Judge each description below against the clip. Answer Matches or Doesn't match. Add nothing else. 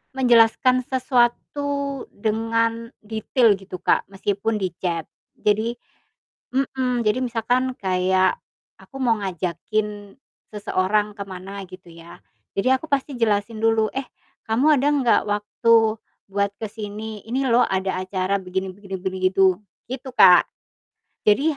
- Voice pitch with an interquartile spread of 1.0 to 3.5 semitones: Doesn't match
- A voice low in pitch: Doesn't match